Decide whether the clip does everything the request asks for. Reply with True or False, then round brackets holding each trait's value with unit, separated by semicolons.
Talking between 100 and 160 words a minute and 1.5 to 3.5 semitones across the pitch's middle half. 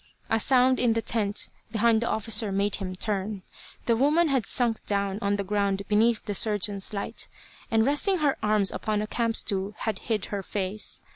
False (190 wpm; 2.6 semitones)